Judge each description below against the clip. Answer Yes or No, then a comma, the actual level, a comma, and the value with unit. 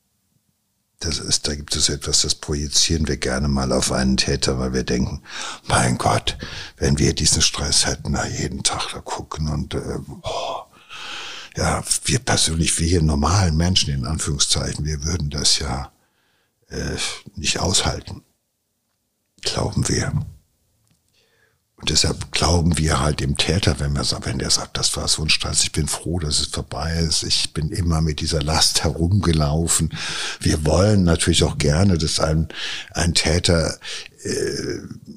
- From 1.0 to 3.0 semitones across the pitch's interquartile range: Yes, narrow, 2.4 semitones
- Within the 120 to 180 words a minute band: Yes, average, 155 wpm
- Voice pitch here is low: Yes, very low, 80 Hz